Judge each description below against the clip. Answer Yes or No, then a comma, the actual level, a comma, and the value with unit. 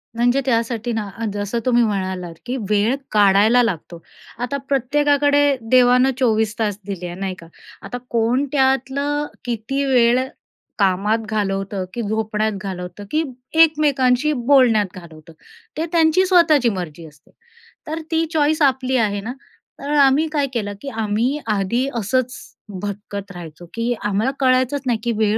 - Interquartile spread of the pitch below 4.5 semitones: No, average, 4.9 semitones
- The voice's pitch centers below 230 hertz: No, high, 235 Hz